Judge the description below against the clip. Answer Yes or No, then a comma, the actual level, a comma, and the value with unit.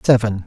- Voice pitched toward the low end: Yes, low, 110 Hz